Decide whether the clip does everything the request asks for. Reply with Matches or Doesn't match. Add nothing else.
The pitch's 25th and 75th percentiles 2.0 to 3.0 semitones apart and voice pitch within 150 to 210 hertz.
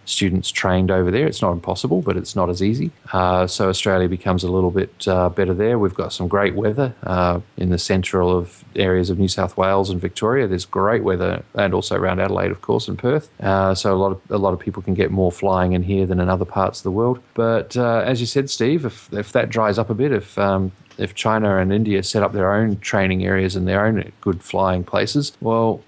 Doesn't match